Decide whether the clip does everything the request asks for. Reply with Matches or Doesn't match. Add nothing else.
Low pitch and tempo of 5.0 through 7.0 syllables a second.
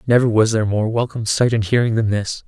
Matches